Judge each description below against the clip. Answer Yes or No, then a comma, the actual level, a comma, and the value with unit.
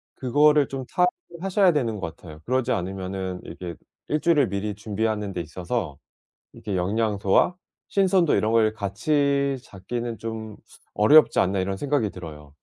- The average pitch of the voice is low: Yes, low, 110 Hz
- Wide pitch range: Yes, wide, 6.7 semitones